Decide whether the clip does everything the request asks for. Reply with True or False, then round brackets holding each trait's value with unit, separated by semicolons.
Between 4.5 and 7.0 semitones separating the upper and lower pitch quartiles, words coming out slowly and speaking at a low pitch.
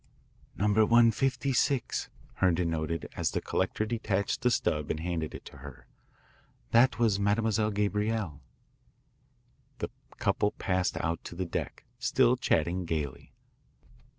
True (5.4 semitones; 125 wpm; 100 Hz)